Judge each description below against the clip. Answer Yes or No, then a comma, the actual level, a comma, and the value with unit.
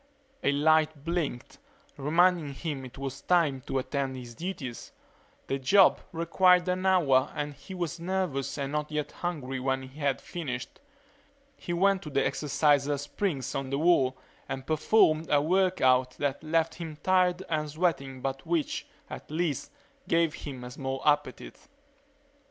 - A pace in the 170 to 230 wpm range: No, average, 155 wpm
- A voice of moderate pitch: Yes, medium, 150 Hz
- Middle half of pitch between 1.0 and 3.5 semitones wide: No, average, 4.2 semitones